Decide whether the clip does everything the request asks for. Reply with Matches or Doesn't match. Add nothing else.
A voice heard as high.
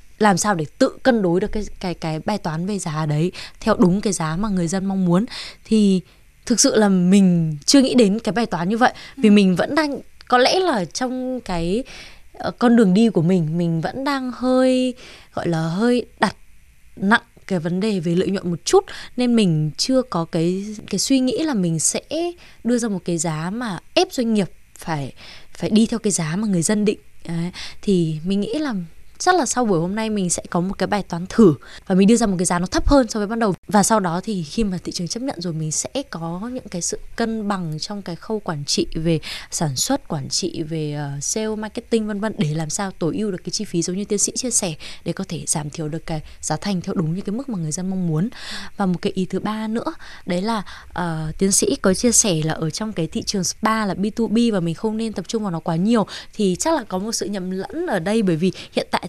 Matches